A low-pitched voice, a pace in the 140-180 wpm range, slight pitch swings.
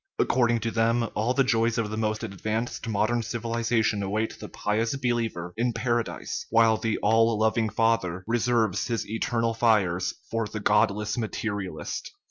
Yes: low, 115 Hz; average, 160 wpm; narrow, 1.6 semitones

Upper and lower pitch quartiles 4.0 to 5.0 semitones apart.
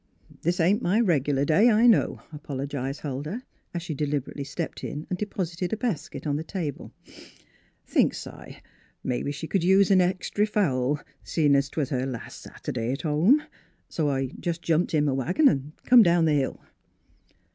Yes: average, 4.7 semitones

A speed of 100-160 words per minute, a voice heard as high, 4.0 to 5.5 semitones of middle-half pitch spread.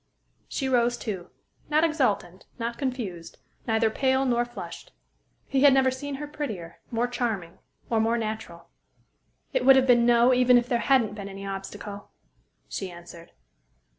Yes: average, 155 wpm; high, 235 Hz; average, 4.5 semitones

